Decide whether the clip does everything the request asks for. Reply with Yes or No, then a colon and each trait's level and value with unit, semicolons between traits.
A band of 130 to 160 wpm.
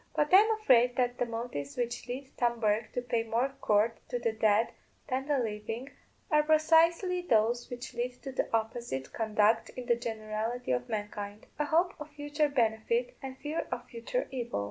No: average, 190 wpm